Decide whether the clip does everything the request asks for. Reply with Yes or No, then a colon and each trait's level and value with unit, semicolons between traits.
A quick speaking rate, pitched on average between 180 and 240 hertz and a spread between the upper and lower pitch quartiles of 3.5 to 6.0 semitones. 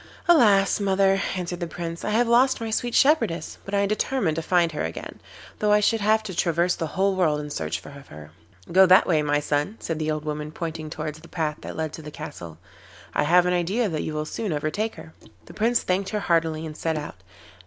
No: fast, 230 wpm; medium, 170 Hz; average, 4.8 semitones